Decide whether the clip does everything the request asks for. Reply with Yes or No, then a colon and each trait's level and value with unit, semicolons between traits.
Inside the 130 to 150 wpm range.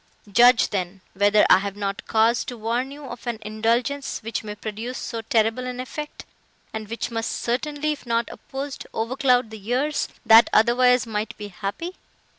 No: average, 170 wpm